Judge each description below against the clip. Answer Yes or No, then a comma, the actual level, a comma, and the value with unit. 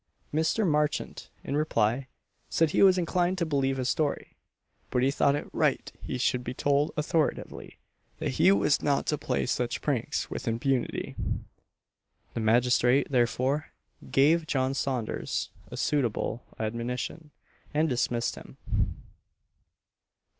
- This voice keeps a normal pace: No, slow, 130 wpm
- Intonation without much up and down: No, average, 3.6 semitones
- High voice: No, low, 135 Hz